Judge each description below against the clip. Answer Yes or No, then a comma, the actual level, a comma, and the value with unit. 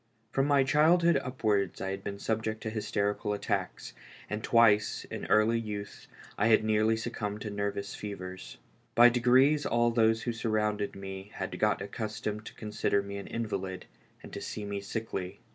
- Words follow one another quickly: No, average, 170 wpm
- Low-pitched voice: Yes, low, 110 Hz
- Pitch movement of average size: No, narrow, 2.3 semitones